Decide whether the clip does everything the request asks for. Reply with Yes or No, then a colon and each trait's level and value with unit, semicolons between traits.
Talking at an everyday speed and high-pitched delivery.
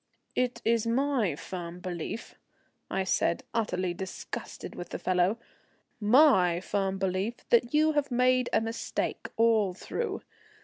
No: slow, 130 wpm; high, 215 Hz